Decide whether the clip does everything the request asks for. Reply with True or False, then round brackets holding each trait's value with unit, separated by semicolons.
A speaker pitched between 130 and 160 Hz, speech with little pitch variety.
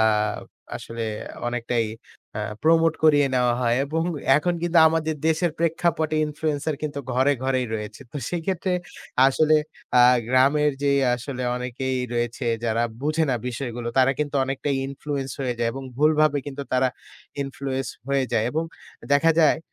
False (140 Hz; 3.7 semitones)